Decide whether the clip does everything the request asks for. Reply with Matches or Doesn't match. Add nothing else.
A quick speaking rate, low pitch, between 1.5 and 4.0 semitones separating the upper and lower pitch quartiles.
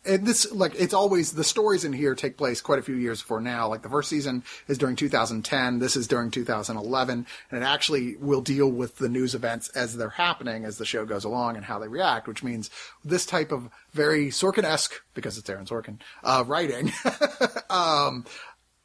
Doesn't match